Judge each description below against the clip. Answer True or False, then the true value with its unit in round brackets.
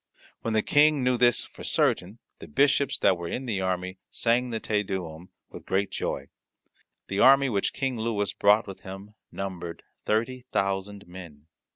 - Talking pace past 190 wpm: False (170 wpm)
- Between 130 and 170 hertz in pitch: False (100 Hz)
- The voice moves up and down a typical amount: True (4.5 semitones)